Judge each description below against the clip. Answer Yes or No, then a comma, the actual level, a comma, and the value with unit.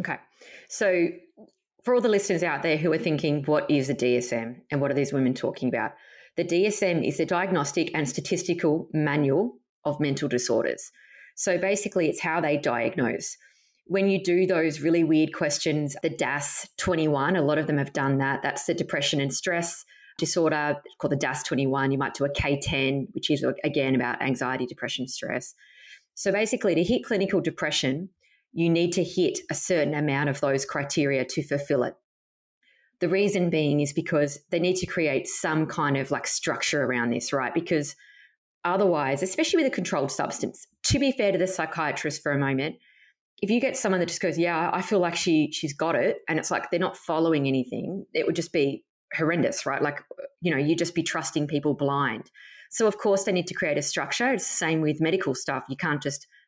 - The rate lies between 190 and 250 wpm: Yes, average, 195 wpm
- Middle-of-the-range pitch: Yes, medium, 155 Hz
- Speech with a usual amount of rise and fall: Yes, average, 4.3 semitones